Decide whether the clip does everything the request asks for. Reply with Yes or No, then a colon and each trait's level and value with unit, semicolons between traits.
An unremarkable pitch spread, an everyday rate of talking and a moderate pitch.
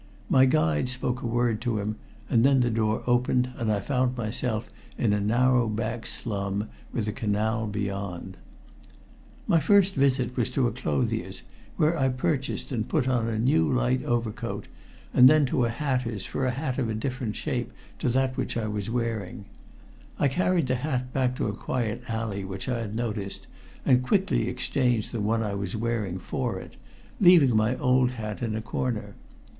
No: average, 3.1 semitones; average, 180 wpm; low, 120 Hz